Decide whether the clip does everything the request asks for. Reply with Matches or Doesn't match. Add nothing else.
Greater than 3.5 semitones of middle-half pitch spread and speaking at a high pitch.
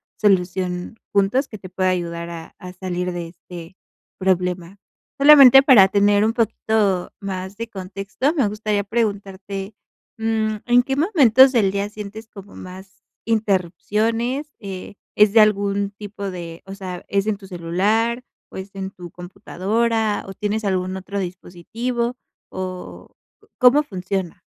Doesn't match